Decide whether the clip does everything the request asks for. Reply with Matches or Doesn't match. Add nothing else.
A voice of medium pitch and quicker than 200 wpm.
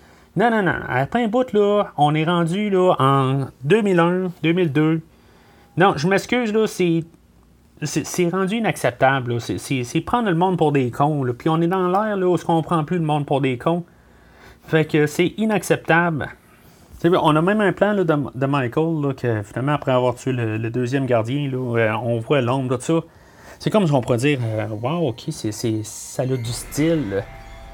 Matches